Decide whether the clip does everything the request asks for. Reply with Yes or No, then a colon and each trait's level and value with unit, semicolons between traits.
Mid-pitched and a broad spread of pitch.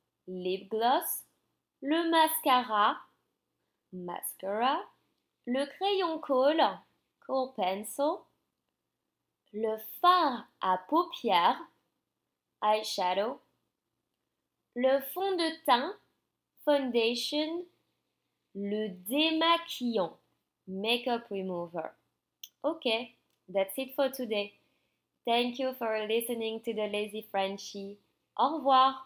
No: high, 240 Hz; wide, 5.8 semitones